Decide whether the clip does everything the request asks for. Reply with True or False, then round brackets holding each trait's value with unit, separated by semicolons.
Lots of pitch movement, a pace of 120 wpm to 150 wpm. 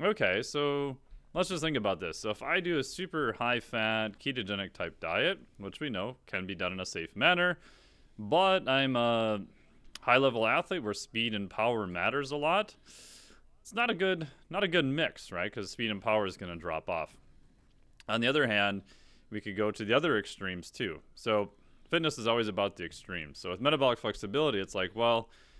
False (6.3 semitones; 195 wpm)